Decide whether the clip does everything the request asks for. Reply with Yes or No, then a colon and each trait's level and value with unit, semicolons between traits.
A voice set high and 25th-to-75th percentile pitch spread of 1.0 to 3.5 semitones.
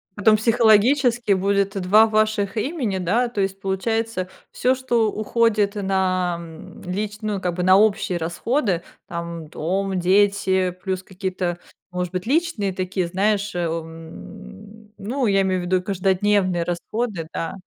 Yes: high, 195 Hz; average, 2.9 semitones